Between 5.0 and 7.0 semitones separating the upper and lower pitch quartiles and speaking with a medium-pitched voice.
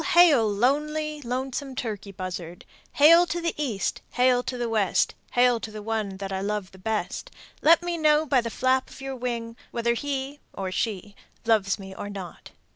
No: wide, 5.6 semitones; high, 235 Hz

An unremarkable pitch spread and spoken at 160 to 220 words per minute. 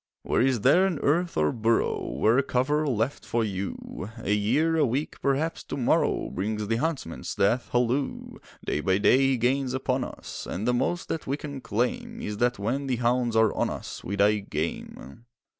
Yes: average, 4.5 semitones; average, 190 wpm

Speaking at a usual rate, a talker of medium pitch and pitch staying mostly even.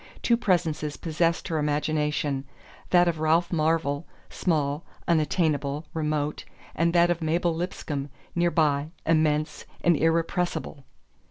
No: slow, 115 wpm; medium, 160 Hz; narrow, 2.2 semitones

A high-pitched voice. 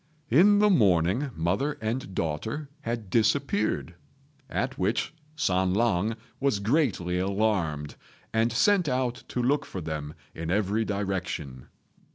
No: low, 105 Hz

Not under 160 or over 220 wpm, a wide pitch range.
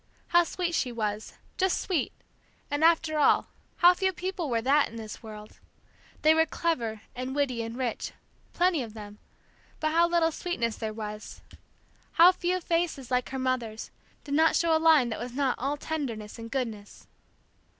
Yes: average, 170 wpm; wide, 6.3 semitones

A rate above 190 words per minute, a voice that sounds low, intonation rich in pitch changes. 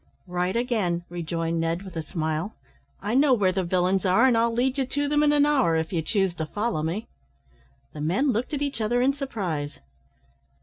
No: fast, 205 wpm; high, 195 Hz; wide, 7.0 semitones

